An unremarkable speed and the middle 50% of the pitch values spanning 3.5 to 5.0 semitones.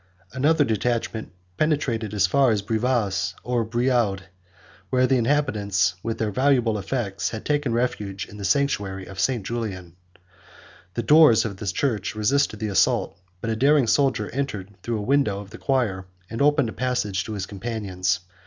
Yes: average, 165 wpm; average, 4.4 semitones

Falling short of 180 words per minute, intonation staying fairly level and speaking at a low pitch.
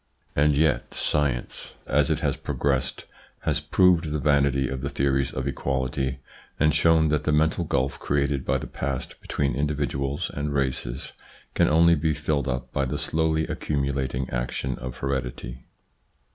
Yes: average, 160 wpm; narrow, 2.3 semitones; very low, 70 Hz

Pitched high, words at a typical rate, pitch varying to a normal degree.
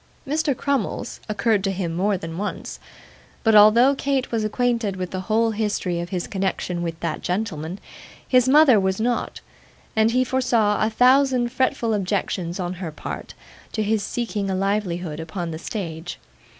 Yes: high, 210 Hz; average, 165 wpm; average, 4.8 semitones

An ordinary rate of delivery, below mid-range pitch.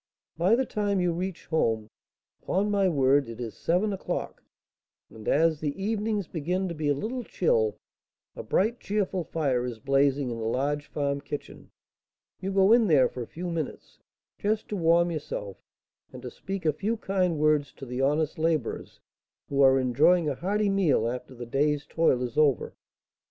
No: average, 180 wpm; medium, 155 Hz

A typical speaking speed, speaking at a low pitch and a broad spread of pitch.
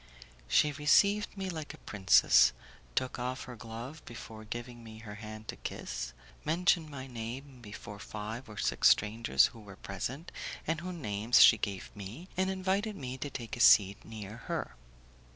Yes: average, 170 wpm; low, 120 Hz; wide, 6.1 semitones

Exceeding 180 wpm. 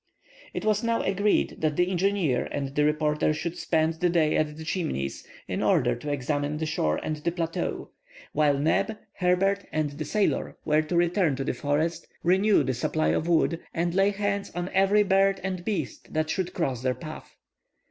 Yes: average, 190 wpm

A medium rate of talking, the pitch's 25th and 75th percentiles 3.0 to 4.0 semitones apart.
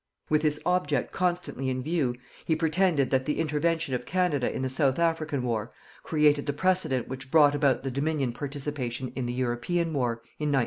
Yes: average, 185 wpm; average, 3.7 semitones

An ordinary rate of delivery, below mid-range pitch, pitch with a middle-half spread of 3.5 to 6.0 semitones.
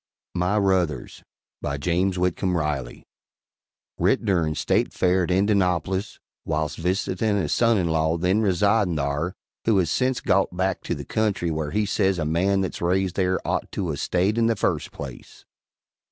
No: average, 160 wpm; very low, 90 Hz; average, 3.0 semitones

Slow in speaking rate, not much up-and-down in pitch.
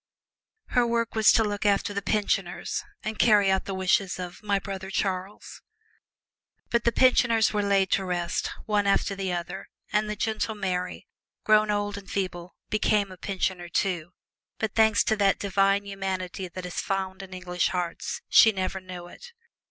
No: average, 175 wpm; narrow, 2.3 semitones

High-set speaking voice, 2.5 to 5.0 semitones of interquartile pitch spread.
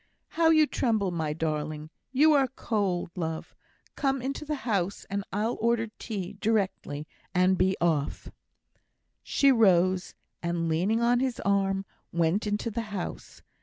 No: high, 200 Hz; wide, 5.4 semitones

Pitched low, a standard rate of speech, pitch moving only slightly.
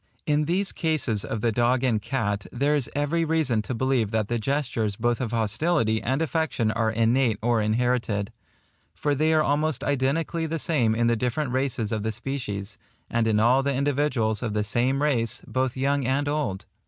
No: low, 125 Hz; average, 190 wpm; average, 4.5 semitones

